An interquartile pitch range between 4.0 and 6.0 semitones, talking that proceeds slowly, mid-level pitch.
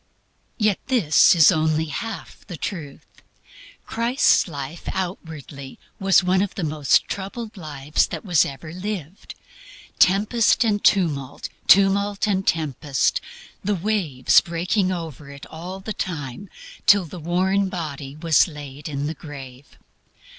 Yes: average, 4.9 semitones; slow, 130 wpm; medium, 170 Hz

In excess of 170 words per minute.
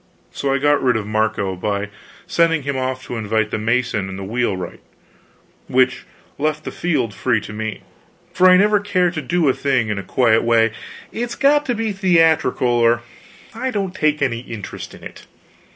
Yes: average, 185 wpm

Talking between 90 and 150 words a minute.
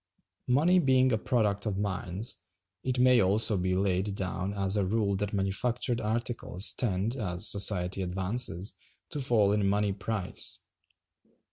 Yes: average, 140 wpm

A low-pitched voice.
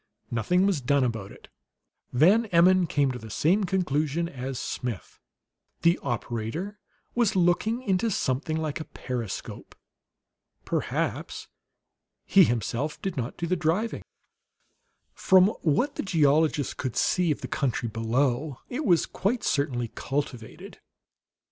No: medium, 155 Hz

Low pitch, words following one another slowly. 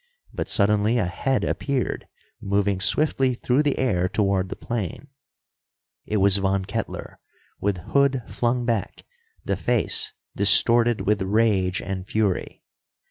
Yes: low, 105 Hz; slow, 130 wpm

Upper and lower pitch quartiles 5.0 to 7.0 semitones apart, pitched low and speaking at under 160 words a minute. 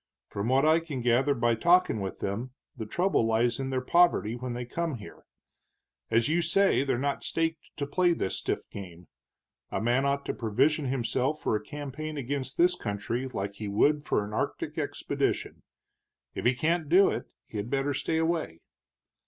No: average, 5.3 semitones; low, 130 Hz; average, 180 wpm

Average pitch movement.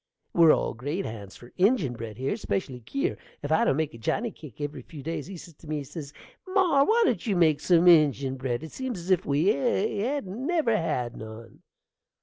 No: wide, 7.4 semitones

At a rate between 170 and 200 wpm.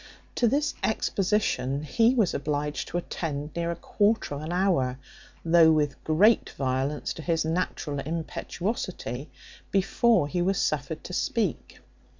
No: average, 140 wpm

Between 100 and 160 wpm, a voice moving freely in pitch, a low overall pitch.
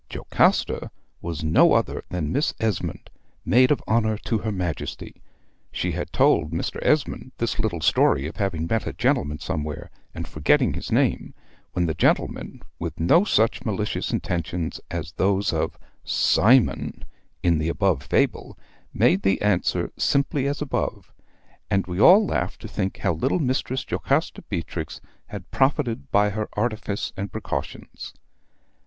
Yes: average, 150 wpm; wide, 5.8 semitones; low, 100 Hz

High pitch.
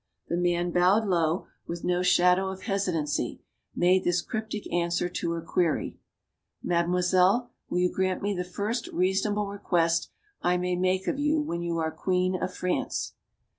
No: medium, 180 Hz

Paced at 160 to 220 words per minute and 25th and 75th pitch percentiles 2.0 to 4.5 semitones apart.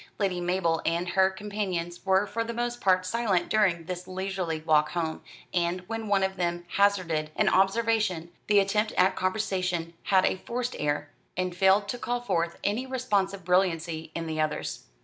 Yes: average, 170 wpm; average, 3.1 semitones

